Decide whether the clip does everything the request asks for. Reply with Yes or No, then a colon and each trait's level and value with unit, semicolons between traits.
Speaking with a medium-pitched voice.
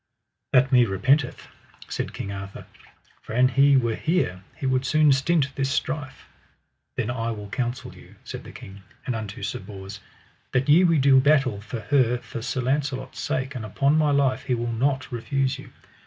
No: low, 130 Hz